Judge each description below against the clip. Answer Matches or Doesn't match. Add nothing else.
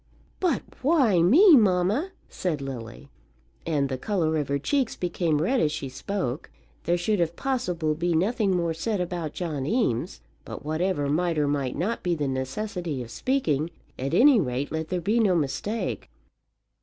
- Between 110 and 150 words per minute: Doesn't match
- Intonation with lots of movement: Matches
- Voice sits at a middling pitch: Matches